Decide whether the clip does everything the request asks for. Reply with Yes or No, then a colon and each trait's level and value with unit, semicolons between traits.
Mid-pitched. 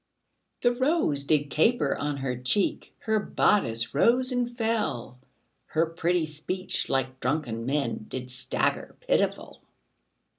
Yes: medium, 155 Hz